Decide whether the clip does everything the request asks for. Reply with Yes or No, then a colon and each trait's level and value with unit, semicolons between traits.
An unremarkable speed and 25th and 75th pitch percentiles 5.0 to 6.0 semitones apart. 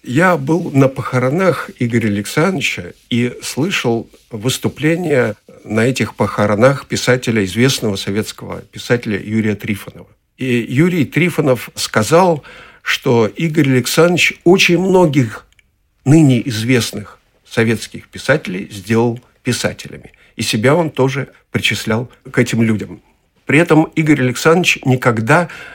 No: slow, 105 wpm; average, 5.3 semitones